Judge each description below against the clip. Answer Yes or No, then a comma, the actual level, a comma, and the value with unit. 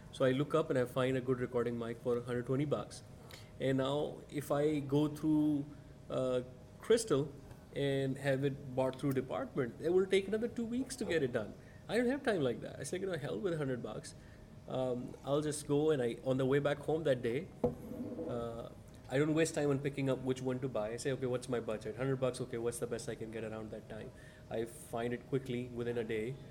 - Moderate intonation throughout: Yes, average, 3.2 semitones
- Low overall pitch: Yes, low, 130 Hz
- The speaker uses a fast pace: Yes, fast, 230 wpm